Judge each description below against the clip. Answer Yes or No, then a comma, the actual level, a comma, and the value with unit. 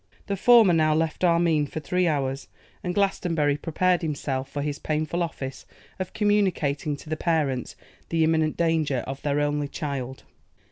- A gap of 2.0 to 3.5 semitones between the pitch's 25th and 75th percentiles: Yes, average, 3.1 semitones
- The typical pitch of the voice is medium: Yes, medium, 155 Hz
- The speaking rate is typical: Yes, average, 155 wpm